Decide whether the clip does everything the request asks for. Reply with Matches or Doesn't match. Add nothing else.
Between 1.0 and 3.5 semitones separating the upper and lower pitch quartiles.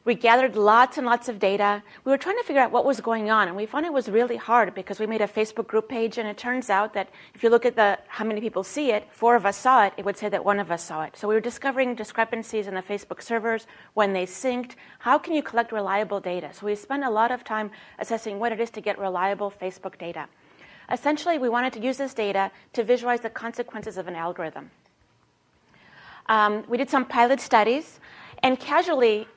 Matches